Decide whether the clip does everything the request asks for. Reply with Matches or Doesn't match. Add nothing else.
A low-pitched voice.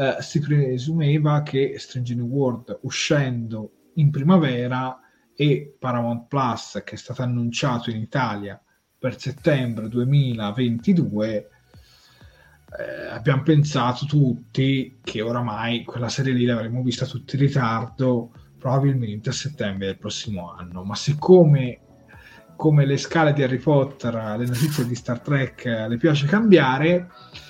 Matches